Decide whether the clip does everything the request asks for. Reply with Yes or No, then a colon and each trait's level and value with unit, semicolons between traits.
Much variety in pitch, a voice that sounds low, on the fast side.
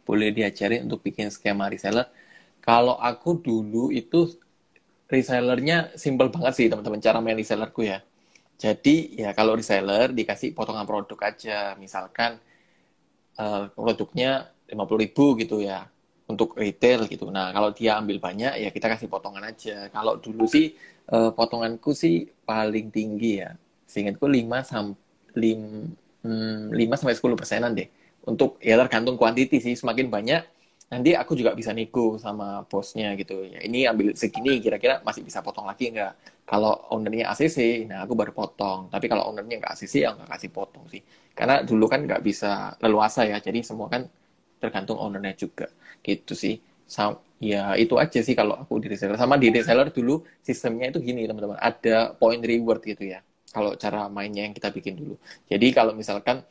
No: narrow, 2.4 semitones; low, 110 Hz; fast, 160 wpm